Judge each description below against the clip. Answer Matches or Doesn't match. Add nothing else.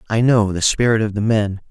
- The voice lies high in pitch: Doesn't match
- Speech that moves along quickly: Matches